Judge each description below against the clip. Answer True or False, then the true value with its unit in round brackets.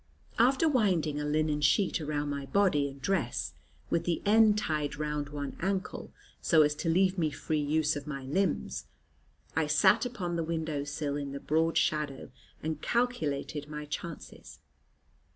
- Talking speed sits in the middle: True (160 wpm)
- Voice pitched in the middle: True (155 Hz)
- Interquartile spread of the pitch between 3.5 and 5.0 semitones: True (4.0 semitones)